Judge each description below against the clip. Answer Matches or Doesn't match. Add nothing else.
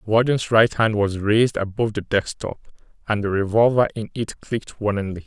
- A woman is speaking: Doesn't match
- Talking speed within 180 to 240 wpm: Matches